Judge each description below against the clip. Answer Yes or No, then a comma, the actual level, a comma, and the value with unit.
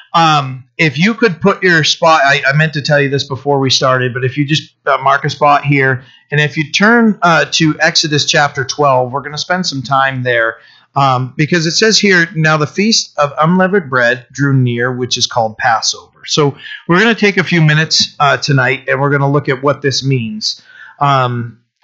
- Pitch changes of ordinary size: Yes, average, 3.4 semitones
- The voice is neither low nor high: Yes, medium, 145 Hz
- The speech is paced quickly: Yes, fast, 215 wpm